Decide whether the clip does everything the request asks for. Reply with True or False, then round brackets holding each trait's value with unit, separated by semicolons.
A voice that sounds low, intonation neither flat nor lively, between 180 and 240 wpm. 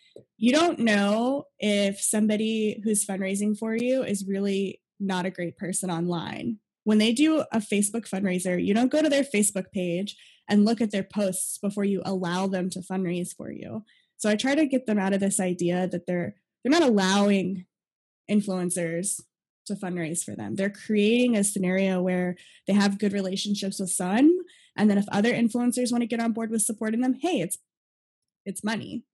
False (205 Hz; 3.3 semitones; 185 wpm)